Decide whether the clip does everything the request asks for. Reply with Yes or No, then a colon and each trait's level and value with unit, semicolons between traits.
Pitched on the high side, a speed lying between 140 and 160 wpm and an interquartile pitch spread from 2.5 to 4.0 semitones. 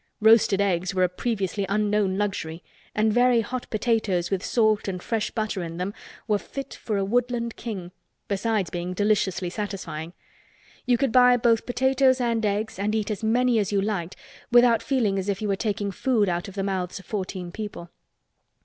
No: high, 210 Hz; average, 180 wpm; average, 3.2 semitones